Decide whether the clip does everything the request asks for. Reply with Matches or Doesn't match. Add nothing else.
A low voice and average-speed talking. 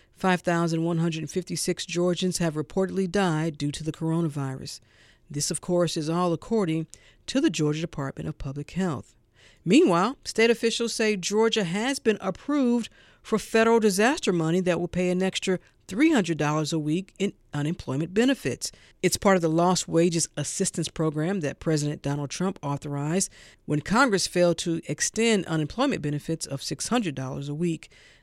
Doesn't match